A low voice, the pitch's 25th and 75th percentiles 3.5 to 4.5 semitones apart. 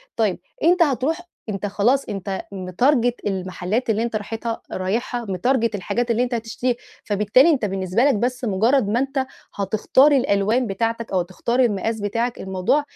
No: high, 225 Hz; average, 4.0 semitones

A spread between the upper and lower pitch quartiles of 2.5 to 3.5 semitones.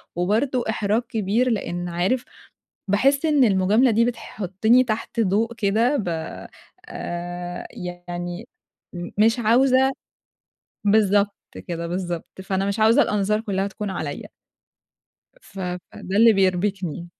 No: average, 4.3 semitones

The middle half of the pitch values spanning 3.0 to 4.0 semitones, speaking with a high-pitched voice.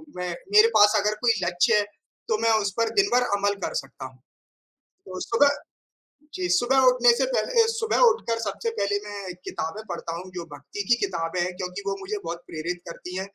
No: average, 4.9 semitones; high, 200 Hz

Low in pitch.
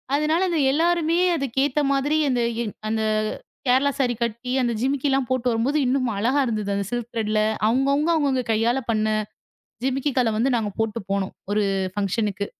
No: very high, 250 Hz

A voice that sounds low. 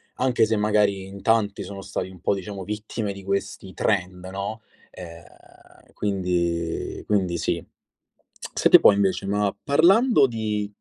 Yes: low, 100 Hz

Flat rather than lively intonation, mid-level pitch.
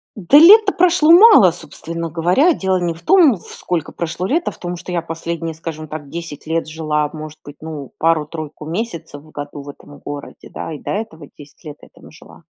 No: average, 3.4 semitones; medium, 165 Hz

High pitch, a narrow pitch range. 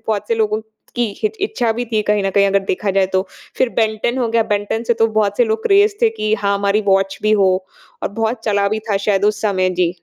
Yes: high, 215 Hz; narrow, 2.2 semitones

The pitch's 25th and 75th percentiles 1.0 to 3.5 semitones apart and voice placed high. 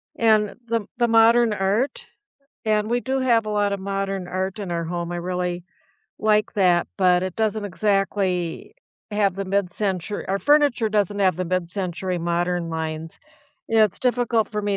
Yes: average, 3.2 semitones; high, 195 Hz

